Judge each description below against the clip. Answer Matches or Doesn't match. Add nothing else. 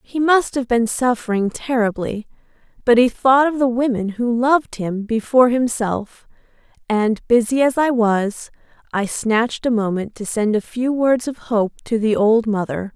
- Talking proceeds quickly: Doesn't match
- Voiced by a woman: Matches